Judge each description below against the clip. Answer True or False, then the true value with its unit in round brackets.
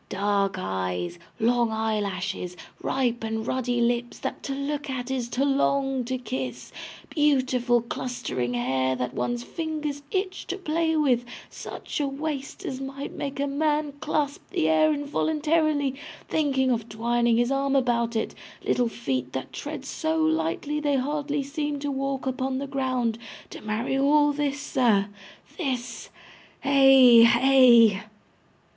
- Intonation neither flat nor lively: True (3.7 semitones)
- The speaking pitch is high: True (260 Hz)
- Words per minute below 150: True (140 wpm)